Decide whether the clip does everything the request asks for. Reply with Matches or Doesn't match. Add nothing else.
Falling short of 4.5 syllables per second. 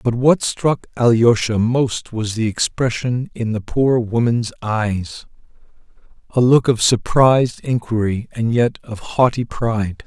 Matches